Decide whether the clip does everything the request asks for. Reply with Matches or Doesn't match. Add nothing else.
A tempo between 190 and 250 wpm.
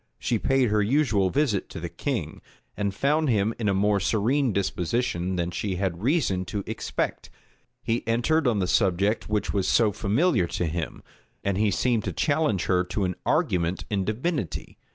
Doesn't match